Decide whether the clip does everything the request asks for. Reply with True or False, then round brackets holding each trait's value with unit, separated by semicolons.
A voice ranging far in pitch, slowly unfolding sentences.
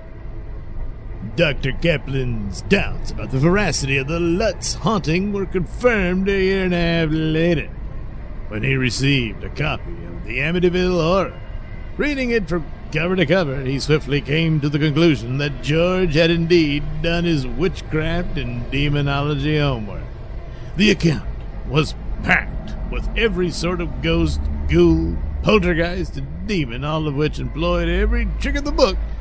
False (5.7 semitones; 145 wpm)